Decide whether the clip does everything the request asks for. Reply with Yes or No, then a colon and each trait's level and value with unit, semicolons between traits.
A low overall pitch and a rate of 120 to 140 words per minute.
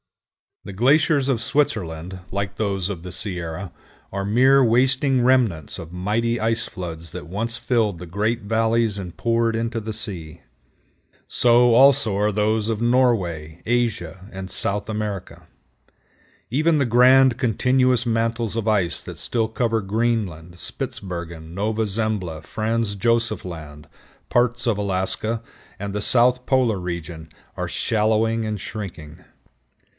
Yes: low, 110 Hz; slow, 135 wpm